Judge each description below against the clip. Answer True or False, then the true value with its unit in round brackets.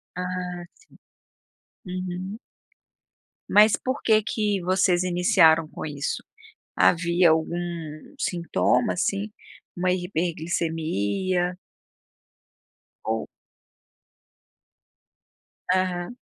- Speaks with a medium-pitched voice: True (180 Hz)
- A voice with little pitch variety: True (1.7 semitones)